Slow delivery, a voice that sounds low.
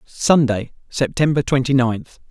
Yes: slow, 105 wpm; low, 130 Hz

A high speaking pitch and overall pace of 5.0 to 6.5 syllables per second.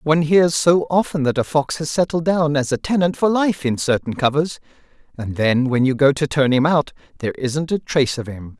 No: medium, 145 Hz; 5.4 syllables/s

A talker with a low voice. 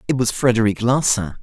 Yes: low, 120 Hz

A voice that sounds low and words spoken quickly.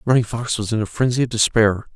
Yes: low, 115 Hz; fast, 245 wpm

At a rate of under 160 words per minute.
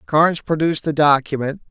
Yes: average, 140 wpm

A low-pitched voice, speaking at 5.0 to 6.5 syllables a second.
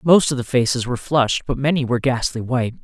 No: low, 130 Hz; 6.9 syllables/s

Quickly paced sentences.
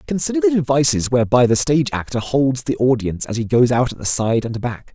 Yes: fast, 230 wpm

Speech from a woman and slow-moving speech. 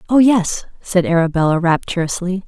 Yes: female; slow, 120 wpm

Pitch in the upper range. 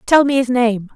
Yes: high, 245 Hz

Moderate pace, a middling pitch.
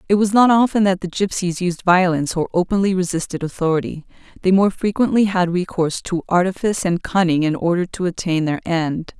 Yes: average, 185 wpm; medium, 180 Hz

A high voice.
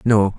No: low, 105 Hz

